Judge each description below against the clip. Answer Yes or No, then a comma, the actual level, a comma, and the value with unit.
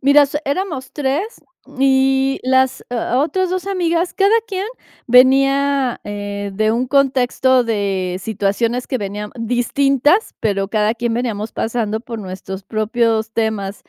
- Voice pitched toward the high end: Yes, high, 245 Hz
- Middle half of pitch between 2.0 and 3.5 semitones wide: No, average, 4.2 semitones